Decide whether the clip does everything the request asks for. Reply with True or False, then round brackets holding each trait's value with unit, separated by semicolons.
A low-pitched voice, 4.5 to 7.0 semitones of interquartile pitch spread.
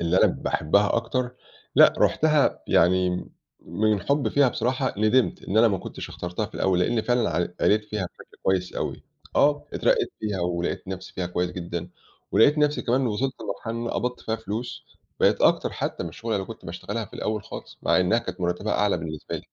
True (105 Hz; 5.1 semitones)